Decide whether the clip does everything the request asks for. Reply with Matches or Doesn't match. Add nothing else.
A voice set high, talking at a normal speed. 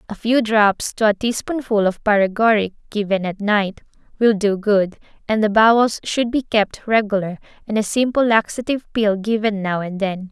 Matches